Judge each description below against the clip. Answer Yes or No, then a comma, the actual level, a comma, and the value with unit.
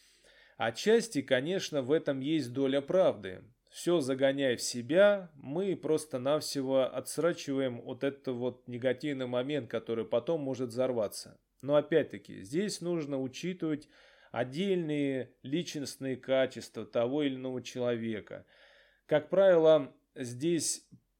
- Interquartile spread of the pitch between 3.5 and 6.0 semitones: Yes, average, 3.8 semitones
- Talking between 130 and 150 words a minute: No, slow, 110 wpm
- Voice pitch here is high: No, medium, 140 Hz